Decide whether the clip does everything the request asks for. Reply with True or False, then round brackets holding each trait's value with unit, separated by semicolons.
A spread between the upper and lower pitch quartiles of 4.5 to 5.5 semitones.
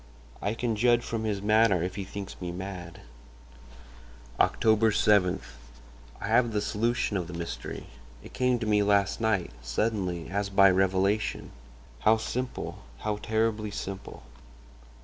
False (3.1 semitones)